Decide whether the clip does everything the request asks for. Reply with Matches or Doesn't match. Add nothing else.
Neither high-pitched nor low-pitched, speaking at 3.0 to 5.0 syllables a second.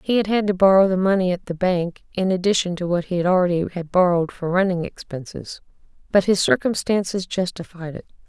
Doesn't match